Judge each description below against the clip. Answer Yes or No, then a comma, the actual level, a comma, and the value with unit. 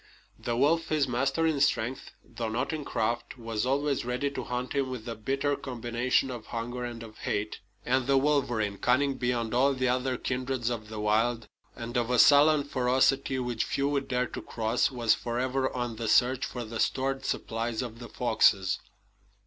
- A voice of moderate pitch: No, low, 125 Hz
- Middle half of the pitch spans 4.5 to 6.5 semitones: No, narrow, 2.5 semitones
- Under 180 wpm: No, average, 185 wpm